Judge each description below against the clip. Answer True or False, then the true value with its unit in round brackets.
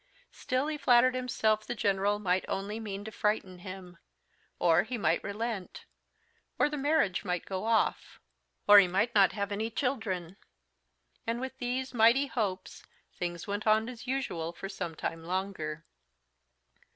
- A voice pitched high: True (205 Hz)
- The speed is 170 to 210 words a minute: False (150 wpm)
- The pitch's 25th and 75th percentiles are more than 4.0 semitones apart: True (4.4 semitones)